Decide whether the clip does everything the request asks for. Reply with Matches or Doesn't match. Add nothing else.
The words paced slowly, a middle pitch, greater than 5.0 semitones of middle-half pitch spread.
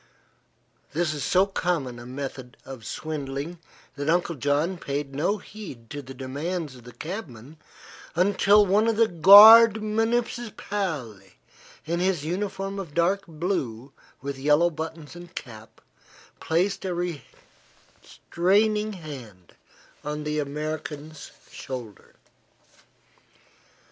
Matches